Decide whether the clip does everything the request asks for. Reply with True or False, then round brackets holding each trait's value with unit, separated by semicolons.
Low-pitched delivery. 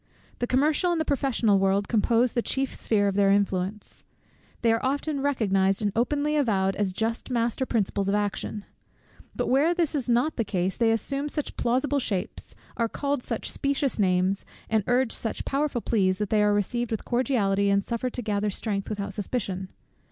False (225 Hz)